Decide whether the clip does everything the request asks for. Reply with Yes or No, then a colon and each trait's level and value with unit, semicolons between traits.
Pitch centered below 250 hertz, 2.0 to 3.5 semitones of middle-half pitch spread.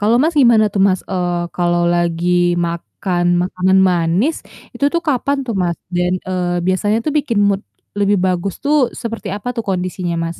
No: medium, 185 Hz; average, 4.1 semitones